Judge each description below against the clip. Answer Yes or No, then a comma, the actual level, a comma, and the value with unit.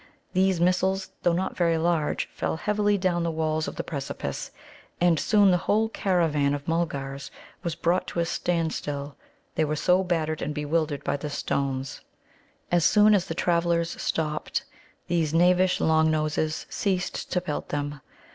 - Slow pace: No, average, 160 wpm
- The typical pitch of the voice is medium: Yes, medium, 165 Hz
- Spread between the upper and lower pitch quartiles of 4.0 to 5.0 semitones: No, average, 2.9 semitones